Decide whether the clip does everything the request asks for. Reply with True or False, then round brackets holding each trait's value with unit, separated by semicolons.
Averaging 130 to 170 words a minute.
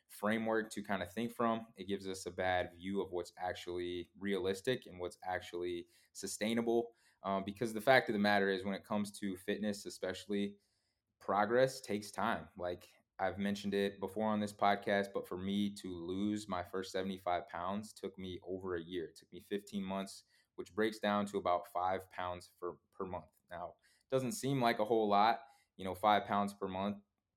False (195 wpm)